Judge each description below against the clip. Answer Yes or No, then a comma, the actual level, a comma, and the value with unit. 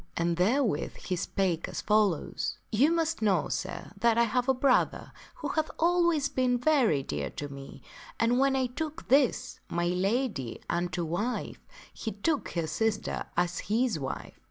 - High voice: Yes, high, 225 Hz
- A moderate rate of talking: Yes, average, 165 wpm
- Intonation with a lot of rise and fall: Yes, wide, 7.4 semitones